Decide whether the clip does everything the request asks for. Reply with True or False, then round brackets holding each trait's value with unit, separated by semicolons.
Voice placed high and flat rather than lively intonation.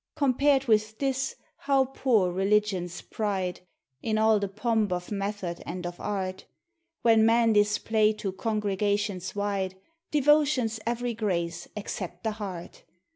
False (210 Hz; 3.3 semitones)